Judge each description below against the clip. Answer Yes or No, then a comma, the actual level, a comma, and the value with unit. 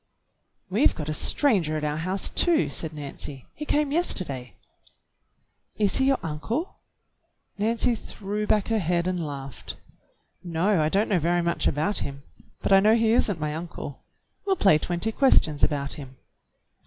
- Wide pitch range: Yes, wide, 6.3 semitones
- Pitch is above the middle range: No, medium, 180 Hz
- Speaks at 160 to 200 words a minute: Yes, average, 165 wpm